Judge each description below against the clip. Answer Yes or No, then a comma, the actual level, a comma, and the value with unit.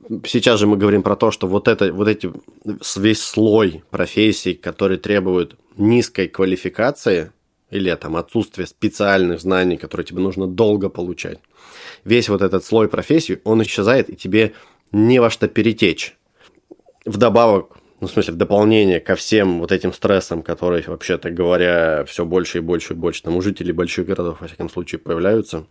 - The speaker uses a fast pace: Yes, fast, 165 wpm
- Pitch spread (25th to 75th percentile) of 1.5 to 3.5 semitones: Yes, average, 3.2 semitones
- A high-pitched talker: No, very low, 95 Hz